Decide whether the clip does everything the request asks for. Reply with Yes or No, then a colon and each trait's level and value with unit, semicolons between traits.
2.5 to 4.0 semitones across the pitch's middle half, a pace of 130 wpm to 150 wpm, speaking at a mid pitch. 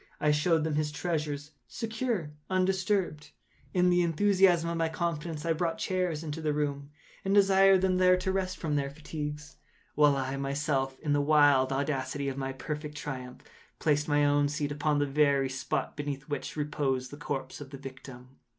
No: average, 3.2 semitones; average, 180 wpm; medium, 150 Hz